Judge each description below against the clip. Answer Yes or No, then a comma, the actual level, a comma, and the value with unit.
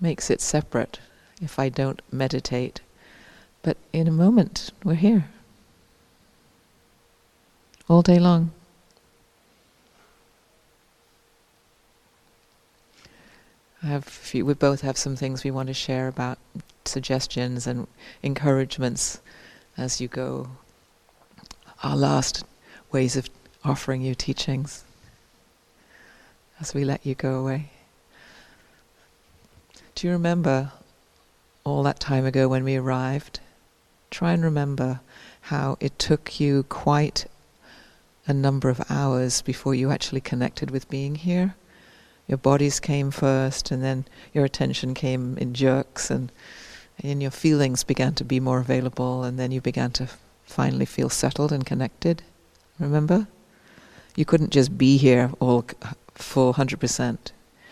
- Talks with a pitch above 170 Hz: No, low, 135 Hz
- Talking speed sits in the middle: No, slow, 120 wpm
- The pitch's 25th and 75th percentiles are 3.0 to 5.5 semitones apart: No, narrow, 2.4 semitones